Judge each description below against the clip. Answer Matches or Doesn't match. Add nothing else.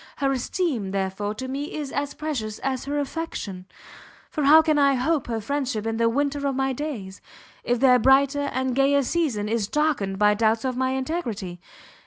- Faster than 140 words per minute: Matches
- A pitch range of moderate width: Matches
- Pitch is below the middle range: Doesn't match